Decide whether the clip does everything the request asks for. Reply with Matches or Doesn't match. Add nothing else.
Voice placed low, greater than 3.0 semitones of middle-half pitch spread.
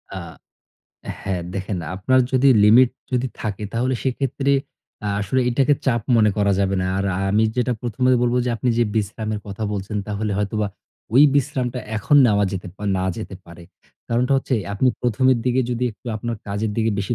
Matches